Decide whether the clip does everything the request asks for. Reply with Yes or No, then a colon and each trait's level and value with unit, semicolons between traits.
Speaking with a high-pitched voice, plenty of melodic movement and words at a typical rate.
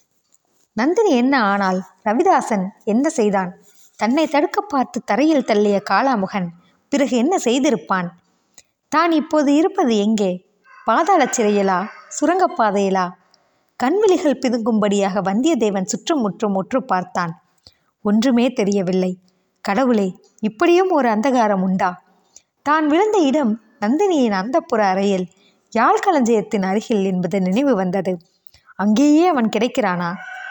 Yes: high, 220 Hz; wide, 6.3 semitones; average, 100 wpm